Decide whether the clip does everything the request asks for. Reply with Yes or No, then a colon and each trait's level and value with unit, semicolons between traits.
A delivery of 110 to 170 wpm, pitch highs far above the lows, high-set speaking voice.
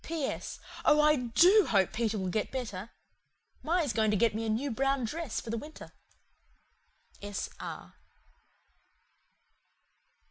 Yes: average, 140 wpm; wide, 5.7 semitones; high, 235 Hz